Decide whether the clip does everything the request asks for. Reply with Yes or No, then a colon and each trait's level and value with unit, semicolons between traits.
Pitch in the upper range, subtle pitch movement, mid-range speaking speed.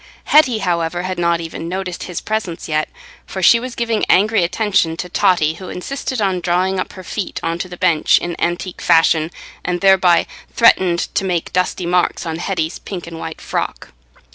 No: medium, 180 Hz; narrow, 2.2 semitones; average, 185 wpm